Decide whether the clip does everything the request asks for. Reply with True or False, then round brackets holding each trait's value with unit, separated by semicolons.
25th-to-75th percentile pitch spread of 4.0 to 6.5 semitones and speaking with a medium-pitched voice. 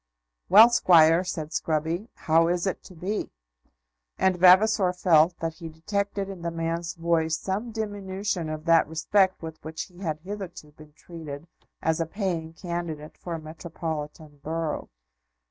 False (2.9 semitones; 170 Hz)